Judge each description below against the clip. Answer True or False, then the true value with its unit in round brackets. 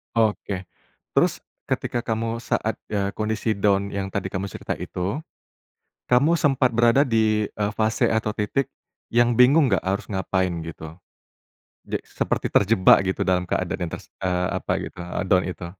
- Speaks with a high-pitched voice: False (105 Hz)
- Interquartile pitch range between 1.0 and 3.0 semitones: False (3.5 semitones)